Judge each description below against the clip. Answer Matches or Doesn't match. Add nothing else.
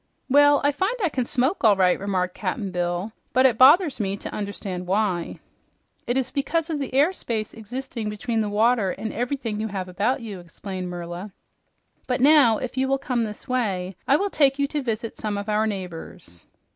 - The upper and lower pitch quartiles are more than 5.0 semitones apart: Matches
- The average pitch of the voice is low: Doesn't match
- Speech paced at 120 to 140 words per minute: Doesn't match